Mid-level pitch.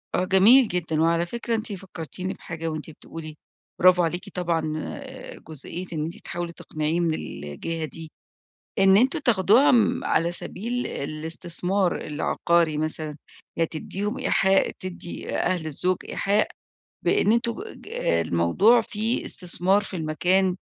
Yes: medium, 175 Hz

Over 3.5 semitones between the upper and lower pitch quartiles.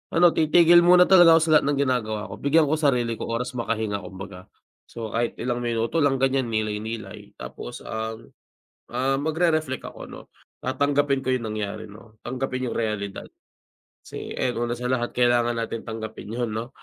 Yes: average, 3.9 semitones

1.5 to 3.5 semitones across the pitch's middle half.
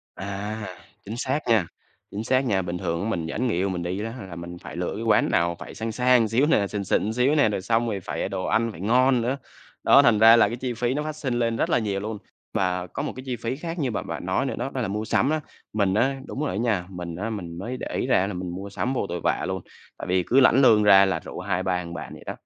No: average, 4.7 semitones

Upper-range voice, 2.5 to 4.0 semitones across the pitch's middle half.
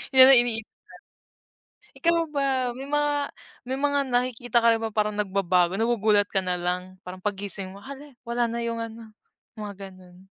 No: high, 220 Hz; average, 4.8 semitones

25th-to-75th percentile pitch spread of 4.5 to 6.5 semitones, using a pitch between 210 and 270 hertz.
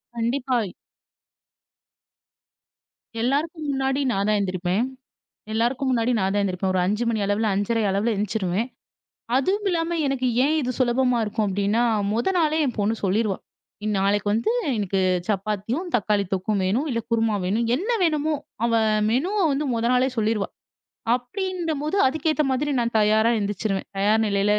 Yes: average, 4.9 semitones; high, 230 Hz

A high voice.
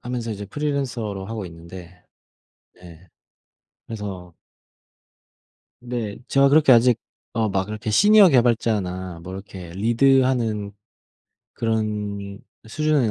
No: low, 110 Hz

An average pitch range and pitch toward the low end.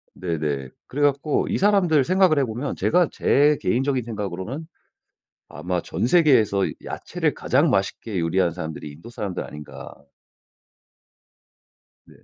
No: wide, 8.6 semitones; low, 115 Hz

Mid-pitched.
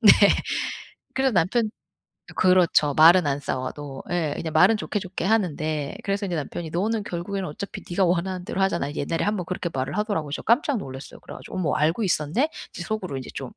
Yes: medium, 175 Hz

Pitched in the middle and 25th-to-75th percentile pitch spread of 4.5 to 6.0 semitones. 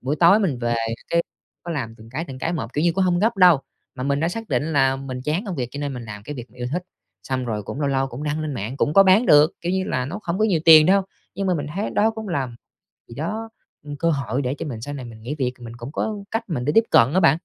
Yes: medium, 145 Hz; wide, 5.6 semitones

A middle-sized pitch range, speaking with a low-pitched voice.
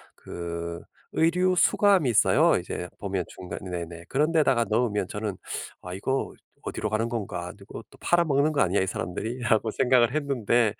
No: wide, 6.8 semitones; low, 110 Hz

